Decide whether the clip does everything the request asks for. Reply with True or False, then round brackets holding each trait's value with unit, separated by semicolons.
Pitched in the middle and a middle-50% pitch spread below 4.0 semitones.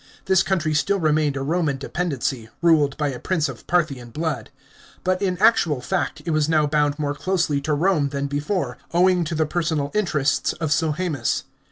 True (155 Hz; 3.5 semitones)